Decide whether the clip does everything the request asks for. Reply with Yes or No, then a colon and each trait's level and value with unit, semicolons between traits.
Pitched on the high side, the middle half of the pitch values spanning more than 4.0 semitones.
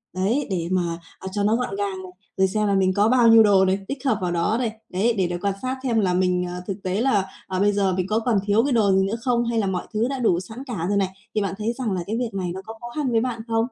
No: high, 205 Hz; average, 3.6 semitones